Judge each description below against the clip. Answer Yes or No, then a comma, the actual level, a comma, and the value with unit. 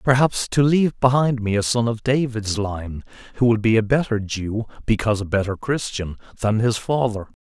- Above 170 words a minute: Yes, average, 185 wpm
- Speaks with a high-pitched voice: No, low, 115 Hz